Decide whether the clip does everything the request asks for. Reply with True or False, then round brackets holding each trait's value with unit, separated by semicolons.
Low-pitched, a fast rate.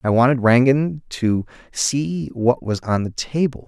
False (125 Hz; 165 wpm)